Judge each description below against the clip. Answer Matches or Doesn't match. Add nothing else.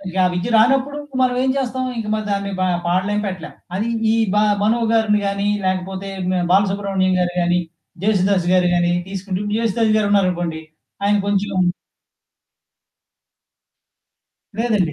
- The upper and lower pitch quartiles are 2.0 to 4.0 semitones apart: Matches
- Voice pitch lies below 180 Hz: Doesn't match